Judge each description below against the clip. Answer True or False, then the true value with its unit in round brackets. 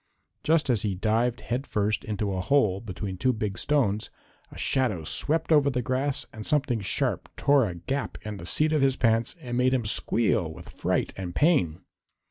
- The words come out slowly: False (190 wpm)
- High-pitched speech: False (115 Hz)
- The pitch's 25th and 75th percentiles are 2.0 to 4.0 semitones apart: False (5.4 semitones)